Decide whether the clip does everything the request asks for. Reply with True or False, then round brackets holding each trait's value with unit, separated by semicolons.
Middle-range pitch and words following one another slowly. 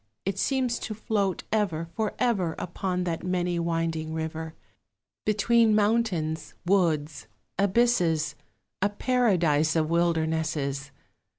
True (175 Hz; 105 wpm)